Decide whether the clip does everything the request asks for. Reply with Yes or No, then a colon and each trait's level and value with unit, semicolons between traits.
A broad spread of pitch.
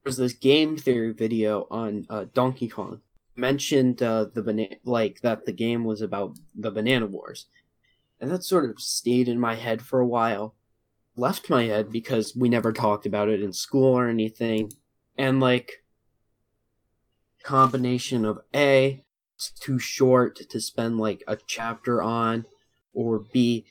No: average, 2.7 semitones